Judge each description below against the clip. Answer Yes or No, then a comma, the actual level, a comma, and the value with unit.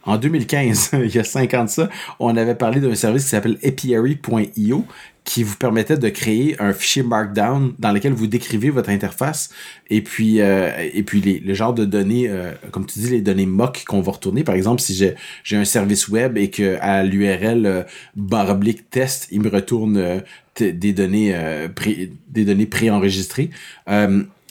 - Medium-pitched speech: No, low, 110 Hz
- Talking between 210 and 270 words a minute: No, average, 190 wpm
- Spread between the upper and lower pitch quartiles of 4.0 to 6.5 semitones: No, average, 3.4 semitones